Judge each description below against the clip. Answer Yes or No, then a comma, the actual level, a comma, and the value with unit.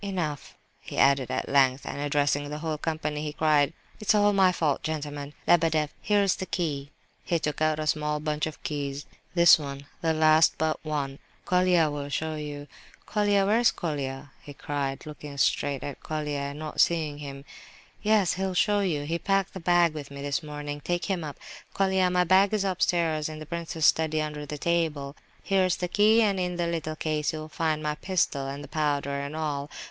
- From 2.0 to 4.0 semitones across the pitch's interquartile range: Yes, average, 3.2 semitones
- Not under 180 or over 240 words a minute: Yes, average, 190 wpm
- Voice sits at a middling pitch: Yes, medium, 155 Hz